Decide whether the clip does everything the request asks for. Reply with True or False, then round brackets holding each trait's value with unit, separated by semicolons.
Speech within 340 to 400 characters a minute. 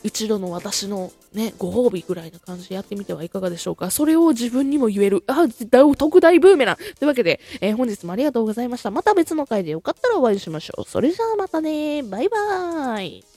False (445 characters per minute)